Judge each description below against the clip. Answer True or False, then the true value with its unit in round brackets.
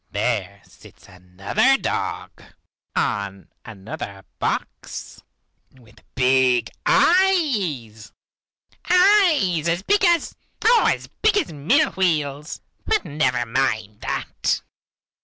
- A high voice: False (145 Hz)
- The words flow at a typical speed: False (95 wpm)